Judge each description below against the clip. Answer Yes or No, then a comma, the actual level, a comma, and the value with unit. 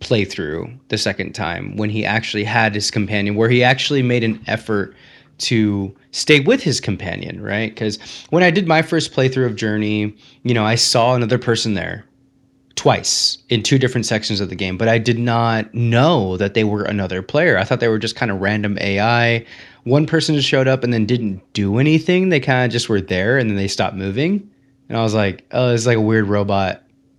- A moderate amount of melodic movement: Yes, average, 3.7 semitones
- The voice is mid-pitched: No, low, 115 Hz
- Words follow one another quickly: Yes, fast, 210 wpm